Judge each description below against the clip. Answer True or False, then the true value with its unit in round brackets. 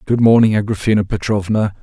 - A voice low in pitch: True (105 Hz)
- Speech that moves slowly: True (130 wpm)